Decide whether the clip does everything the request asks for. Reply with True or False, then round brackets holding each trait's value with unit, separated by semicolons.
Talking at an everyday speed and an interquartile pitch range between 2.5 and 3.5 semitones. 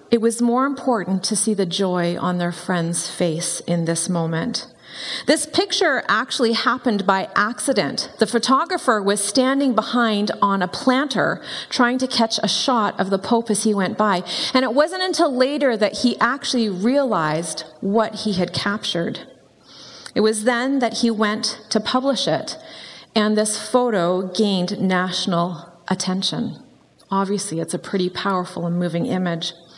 False (155 wpm; 5.3 semitones)